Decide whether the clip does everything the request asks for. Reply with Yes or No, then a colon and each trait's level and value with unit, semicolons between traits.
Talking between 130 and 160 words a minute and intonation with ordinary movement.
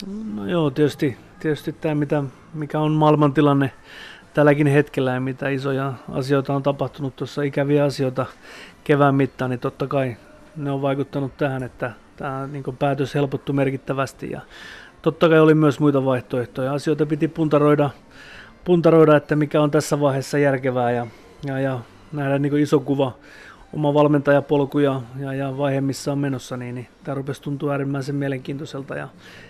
No: fast, 155 wpm; narrow, 1.6 semitones